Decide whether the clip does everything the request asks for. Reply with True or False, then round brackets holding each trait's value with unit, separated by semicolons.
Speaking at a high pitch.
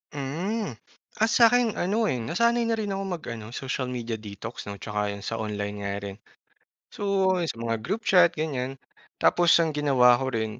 False (135 Hz)